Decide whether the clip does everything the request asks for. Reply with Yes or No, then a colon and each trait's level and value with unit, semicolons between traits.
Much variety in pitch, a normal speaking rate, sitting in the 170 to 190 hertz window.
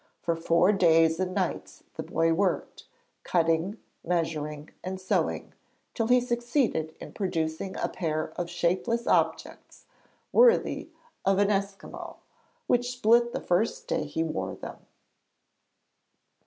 No: wide, 5.7 semitones; slow, 125 wpm; medium, 185 Hz